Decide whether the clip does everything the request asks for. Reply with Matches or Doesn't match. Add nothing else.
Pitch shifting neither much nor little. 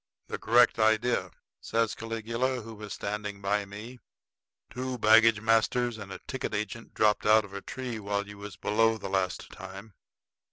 Doesn't match